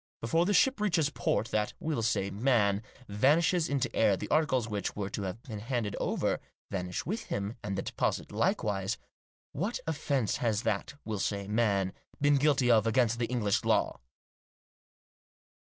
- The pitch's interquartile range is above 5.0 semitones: Yes, wide, 5.6 semitones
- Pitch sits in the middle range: No, low, 115 Hz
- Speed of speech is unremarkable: Yes, average, 160 wpm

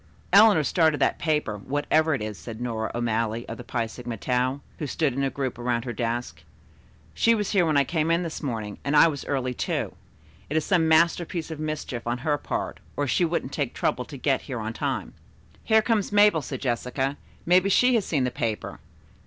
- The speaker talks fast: Yes, fast, 210 wpm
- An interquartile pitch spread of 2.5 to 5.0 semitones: No, wide, 5.4 semitones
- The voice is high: No, medium, 140 Hz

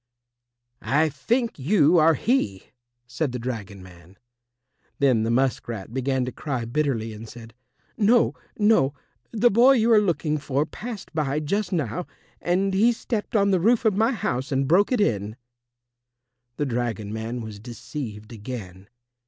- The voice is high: No, medium, 140 Hz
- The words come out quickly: No, average, 155 wpm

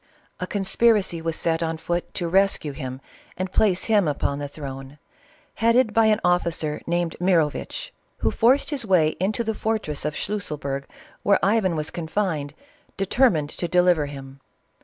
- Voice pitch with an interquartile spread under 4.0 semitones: No, wide, 5.4 semitones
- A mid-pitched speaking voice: Yes, medium, 175 Hz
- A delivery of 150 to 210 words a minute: Yes, average, 160 wpm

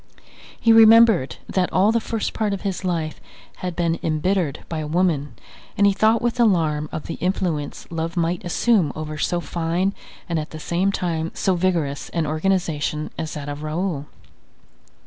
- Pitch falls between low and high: Yes, medium, 170 Hz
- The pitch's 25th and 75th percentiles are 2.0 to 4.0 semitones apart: Yes, average, 3.7 semitones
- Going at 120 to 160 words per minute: No, average, 170 wpm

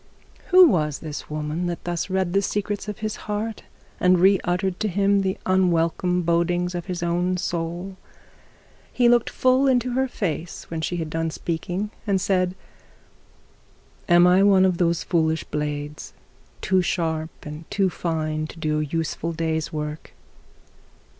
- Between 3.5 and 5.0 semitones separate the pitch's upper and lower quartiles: No, average, 3.1 semitones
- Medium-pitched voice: Yes, medium, 175 Hz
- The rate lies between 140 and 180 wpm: Yes, average, 155 wpm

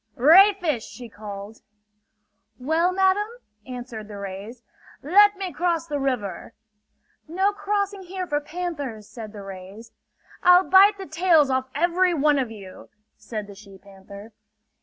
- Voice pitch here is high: Yes, very high, 285 Hz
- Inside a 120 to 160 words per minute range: Yes, average, 140 wpm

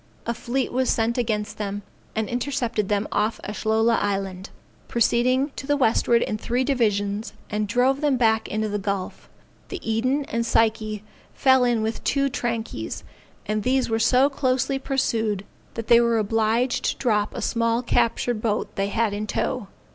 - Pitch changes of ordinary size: Yes, average, 3.0 semitones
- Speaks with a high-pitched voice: Yes, high, 230 Hz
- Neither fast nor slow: Yes, average, 165 wpm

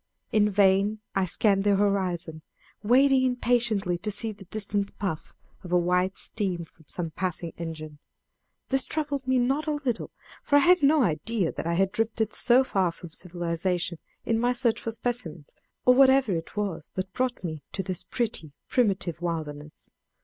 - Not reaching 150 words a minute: No, average, 165 wpm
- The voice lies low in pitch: No, high, 195 Hz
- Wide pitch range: Yes, wide, 5.8 semitones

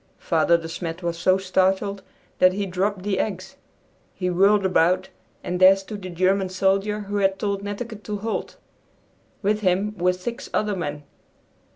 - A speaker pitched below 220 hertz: Yes, high, 190 Hz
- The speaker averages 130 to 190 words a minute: Yes, average, 165 wpm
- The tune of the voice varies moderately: No, narrow, 1.9 semitones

